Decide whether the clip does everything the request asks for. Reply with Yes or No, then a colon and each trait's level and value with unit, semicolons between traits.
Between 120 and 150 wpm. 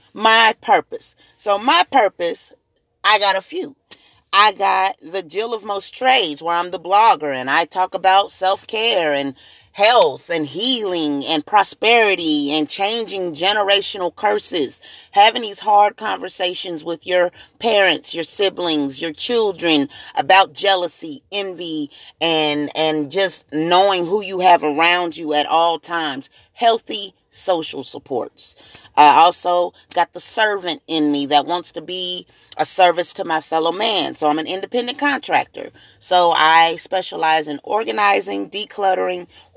Yes: average, 140 wpm